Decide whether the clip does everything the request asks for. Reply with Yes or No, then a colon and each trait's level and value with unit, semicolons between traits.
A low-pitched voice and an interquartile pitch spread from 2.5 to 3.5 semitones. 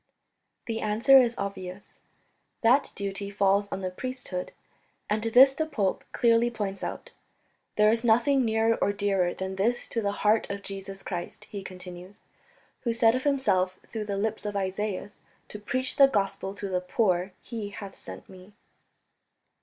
No: high, 205 Hz; average, 3.0 semitones